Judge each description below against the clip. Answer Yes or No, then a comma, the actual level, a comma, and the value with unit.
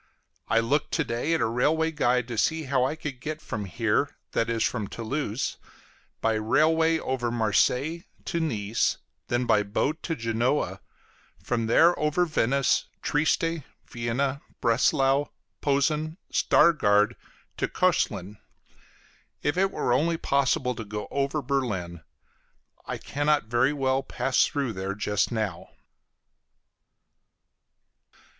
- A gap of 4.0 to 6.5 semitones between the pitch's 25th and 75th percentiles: Yes, average, 4.9 semitones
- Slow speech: Yes, slow, 125 wpm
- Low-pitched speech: Yes, low, 130 Hz